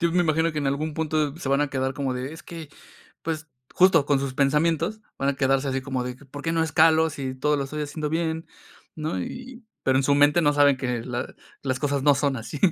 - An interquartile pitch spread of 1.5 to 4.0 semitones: Yes, average, 2.9 semitones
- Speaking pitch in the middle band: Yes, medium, 145 Hz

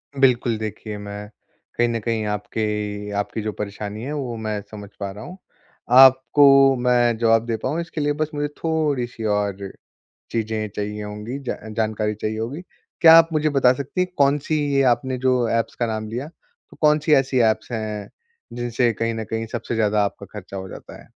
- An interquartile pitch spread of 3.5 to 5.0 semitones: Yes, average, 4.2 semitones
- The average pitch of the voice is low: Yes, low, 115 Hz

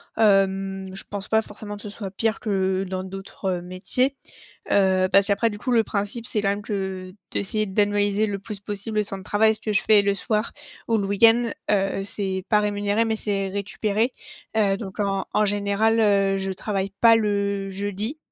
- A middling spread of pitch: No, narrow, 1.6 semitones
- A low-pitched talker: No, high, 200 Hz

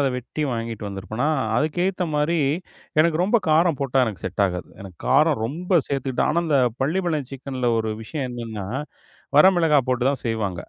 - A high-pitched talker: No, low, 135 Hz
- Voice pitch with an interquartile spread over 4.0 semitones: Yes, wide, 5.6 semitones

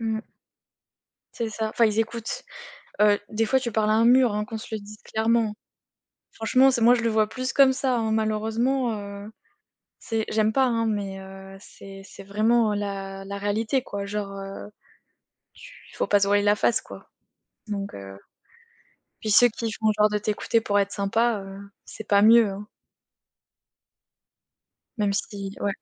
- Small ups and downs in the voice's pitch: Yes, narrow, 2.1 semitones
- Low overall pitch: No, high, 215 Hz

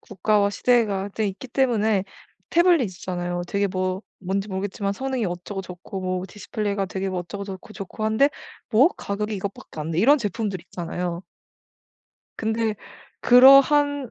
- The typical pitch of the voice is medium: No, high, 200 Hz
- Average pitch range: Yes, average, 3.5 semitones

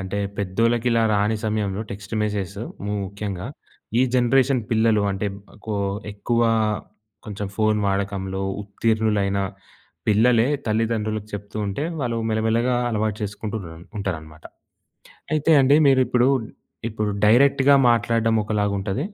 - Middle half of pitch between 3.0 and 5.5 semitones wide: No, narrow, 2.5 semitones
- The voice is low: Yes, low, 110 Hz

